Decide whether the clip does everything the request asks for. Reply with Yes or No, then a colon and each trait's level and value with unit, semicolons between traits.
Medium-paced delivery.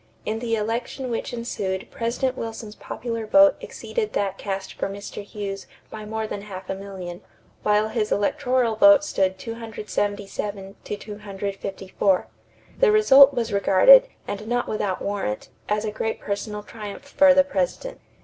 Yes: average, 150 wpm